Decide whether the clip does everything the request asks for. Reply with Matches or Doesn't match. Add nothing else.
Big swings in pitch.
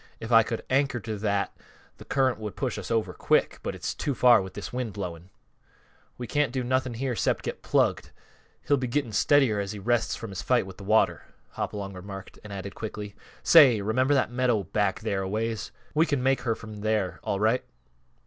Doesn't match